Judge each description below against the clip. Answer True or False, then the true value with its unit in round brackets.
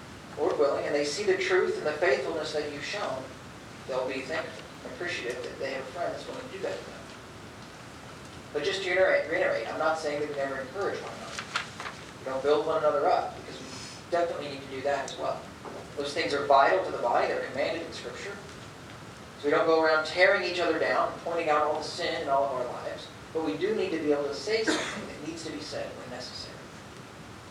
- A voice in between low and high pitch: True (155 Hz)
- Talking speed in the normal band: False (230 wpm)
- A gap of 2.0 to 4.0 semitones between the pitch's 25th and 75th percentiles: True (3.0 semitones)